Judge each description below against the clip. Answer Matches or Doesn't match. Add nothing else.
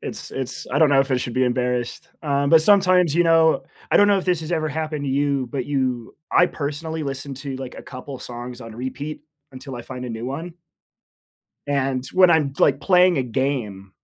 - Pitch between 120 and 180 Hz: Matches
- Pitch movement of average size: Matches